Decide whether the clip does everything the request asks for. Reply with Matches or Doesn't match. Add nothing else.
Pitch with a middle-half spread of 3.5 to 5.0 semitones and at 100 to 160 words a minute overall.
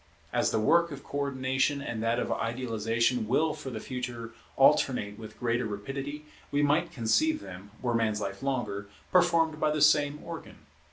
Doesn't match